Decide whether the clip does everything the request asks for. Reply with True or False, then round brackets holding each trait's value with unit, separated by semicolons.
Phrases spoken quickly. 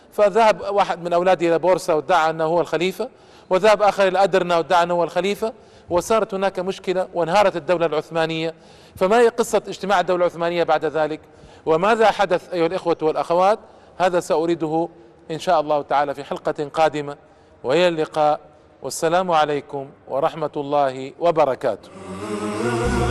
True (140 wpm)